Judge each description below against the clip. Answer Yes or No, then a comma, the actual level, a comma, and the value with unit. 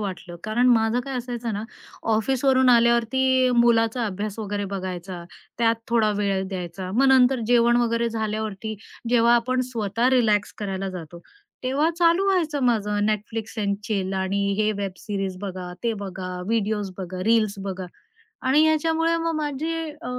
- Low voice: No, high, 225 Hz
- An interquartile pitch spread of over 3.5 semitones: Yes, average, 4.0 semitones